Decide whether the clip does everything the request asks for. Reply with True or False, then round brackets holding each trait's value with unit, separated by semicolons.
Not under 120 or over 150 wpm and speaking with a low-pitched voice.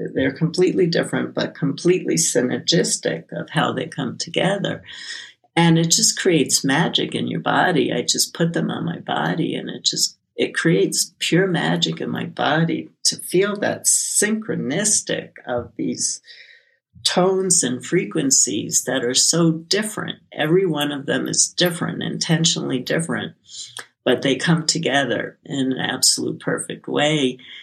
False (145 wpm; 165 Hz)